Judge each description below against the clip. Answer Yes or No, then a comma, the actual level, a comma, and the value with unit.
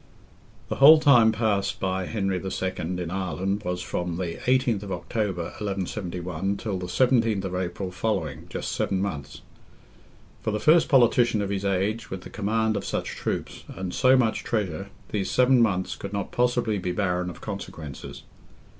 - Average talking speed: Yes, average, 165 wpm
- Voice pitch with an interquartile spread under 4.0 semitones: Yes, average, 3.5 semitones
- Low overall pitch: Yes, low, 100 Hz